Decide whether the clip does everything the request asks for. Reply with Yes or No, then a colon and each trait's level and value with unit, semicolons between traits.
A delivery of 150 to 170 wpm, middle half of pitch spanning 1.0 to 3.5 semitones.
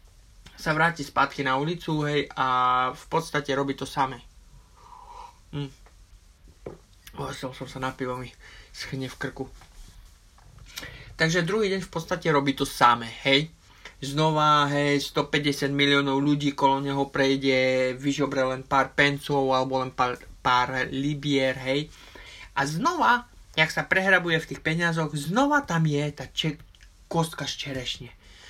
No: average, 140 wpm; average, 2.8 semitones